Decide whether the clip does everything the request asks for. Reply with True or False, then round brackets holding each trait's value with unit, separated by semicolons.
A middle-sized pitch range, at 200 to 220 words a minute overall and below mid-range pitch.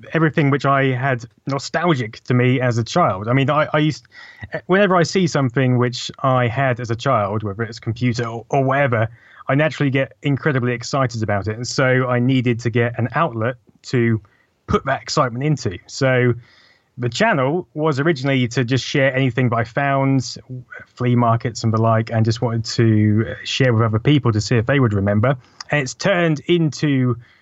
False (3.1 semitones; 190 wpm; 125 Hz)